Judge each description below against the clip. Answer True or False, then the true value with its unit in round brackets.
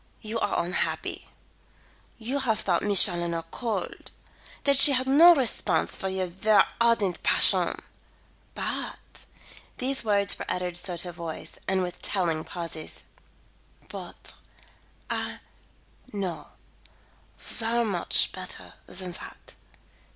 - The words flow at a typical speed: False (120 wpm)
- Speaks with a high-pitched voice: True (195 Hz)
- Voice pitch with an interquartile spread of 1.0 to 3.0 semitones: False (4.8 semitones)